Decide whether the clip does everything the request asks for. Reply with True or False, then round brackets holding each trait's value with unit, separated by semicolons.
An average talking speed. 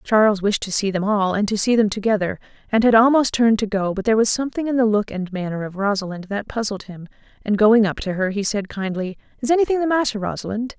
False (245 wpm)